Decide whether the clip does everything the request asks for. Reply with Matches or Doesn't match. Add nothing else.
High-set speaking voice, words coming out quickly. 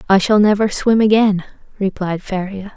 Doesn't match